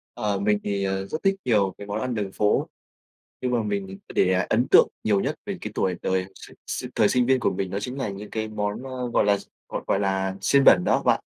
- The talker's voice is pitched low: Yes, low, 105 Hz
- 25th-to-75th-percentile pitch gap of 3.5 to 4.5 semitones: Yes, average, 4.0 semitones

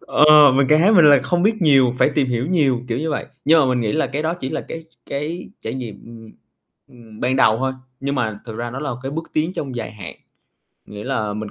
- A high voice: No, low, 135 Hz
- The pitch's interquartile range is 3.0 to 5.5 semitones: Yes, average, 4.6 semitones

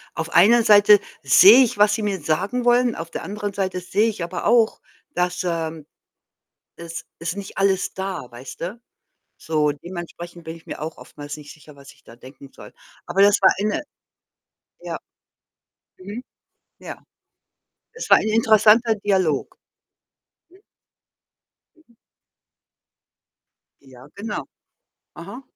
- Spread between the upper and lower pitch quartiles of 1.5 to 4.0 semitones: No, average, 4.7 semitones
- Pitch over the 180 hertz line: Yes, high, 190 Hz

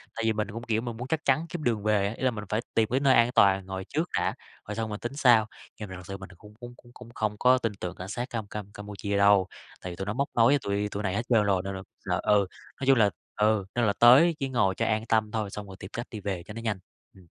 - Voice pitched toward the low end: Yes, low, 110 Hz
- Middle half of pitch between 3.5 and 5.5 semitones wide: No, average, 3.0 semitones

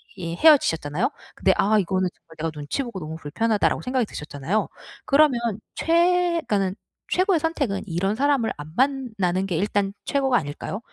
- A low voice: No, high, 205 Hz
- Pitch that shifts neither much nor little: No, wide, 8.1 semitones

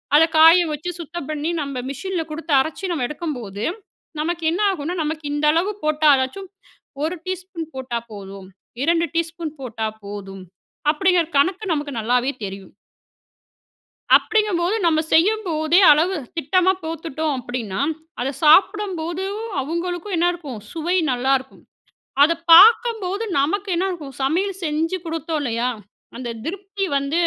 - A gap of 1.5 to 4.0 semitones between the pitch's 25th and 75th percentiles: No, average, 4.8 semitones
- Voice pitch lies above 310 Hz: Yes, very high, 320 Hz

